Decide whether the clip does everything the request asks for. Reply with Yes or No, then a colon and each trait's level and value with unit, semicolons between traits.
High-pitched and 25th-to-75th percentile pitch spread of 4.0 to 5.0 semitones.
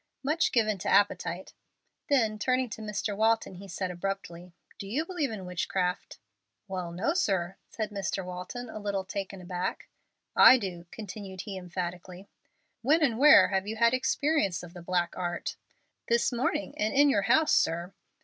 Yes: high, 195 Hz; average, 4.3 semitones